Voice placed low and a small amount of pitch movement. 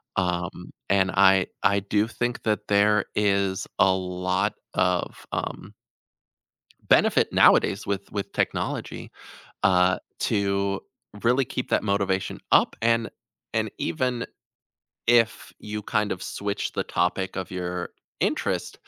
Yes: low, 100 Hz; narrow, 2.2 semitones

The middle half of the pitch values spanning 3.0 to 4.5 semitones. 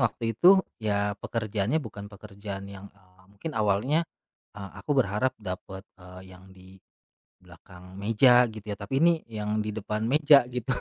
Yes: average, 3.5 semitones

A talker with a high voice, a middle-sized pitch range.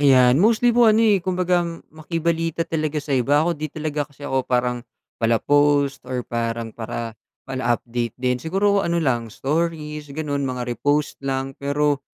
No: medium, 145 Hz; average, 4.6 semitones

